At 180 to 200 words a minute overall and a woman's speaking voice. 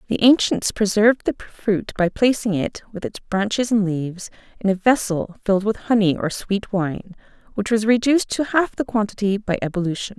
Yes: average, 185 wpm; female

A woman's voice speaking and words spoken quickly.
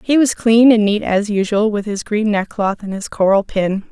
Yes: female; fast, 230 wpm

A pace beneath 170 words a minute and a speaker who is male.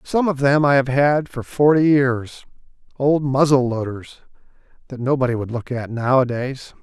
Yes: average, 160 wpm; male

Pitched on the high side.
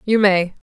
Yes: high, 195 Hz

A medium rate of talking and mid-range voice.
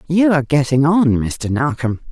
Yes: average, 170 wpm; medium, 145 Hz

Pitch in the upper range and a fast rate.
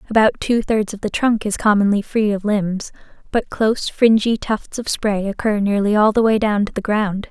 Yes: high, 210 Hz; fast, 215 wpm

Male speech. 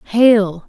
No: female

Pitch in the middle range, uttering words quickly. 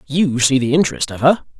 Yes: medium, 145 Hz; fast, 225 wpm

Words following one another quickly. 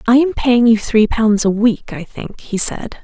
Yes: fast, 240 wpm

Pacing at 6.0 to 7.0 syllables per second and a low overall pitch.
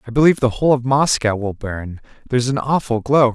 Yes: 6.1 syllables/s; low, 125 Hz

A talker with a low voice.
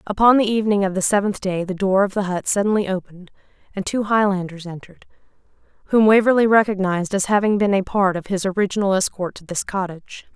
No: high, 195 Hz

